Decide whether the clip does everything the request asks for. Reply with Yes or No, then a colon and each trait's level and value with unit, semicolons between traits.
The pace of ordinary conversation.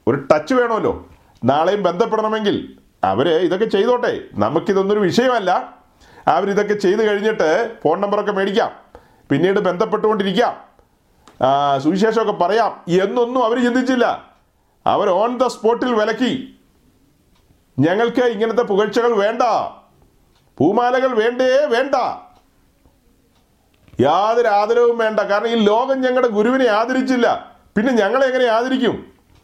Yes: average, 95 wpm